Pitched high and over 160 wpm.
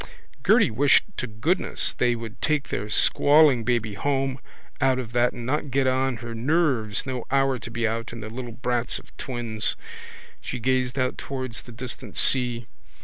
No: low, 125 Hz; average, 175 wpm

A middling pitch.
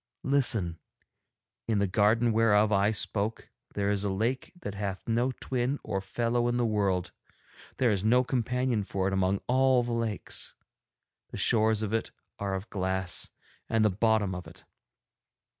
No: low, 110 Hz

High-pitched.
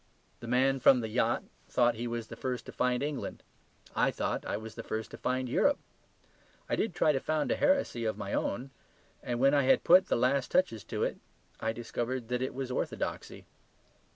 No: low, 125 Hz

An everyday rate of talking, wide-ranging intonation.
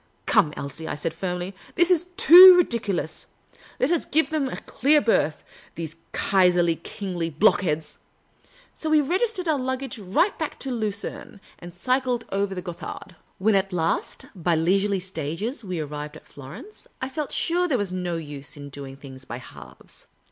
Yes: average, 175 wpm; wide, 8.4 semitones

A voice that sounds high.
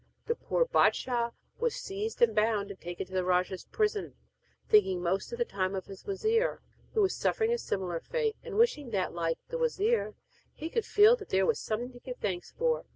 Yes: very high, 250 Hz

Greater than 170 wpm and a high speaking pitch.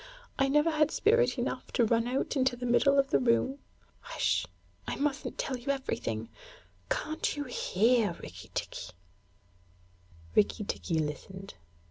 No: average, 140 wpm; very high, 255 Hz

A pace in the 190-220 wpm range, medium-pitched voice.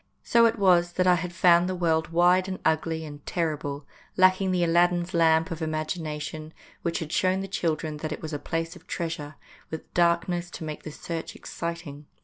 Yes: average, 195 wpm; medium, 170 Hz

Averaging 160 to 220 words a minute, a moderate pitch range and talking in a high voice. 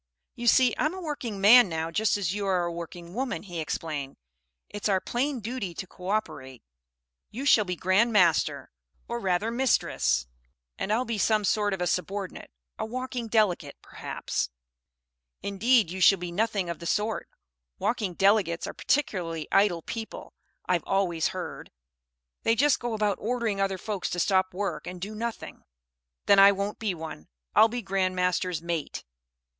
Yes: average, 170 wpm; average, 4.1 semitones; high, 195 Hz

